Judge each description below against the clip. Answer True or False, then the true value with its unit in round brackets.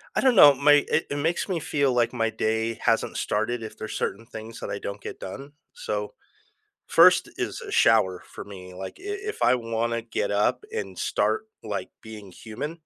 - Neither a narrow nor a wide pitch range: False (5.7 semitones)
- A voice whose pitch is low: True (115 Hz)